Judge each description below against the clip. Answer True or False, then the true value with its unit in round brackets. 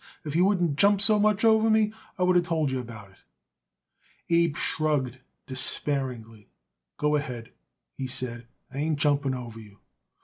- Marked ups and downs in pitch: True (5.9 semitones)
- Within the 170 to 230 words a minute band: False (160 wpm)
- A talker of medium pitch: True (145 Hz)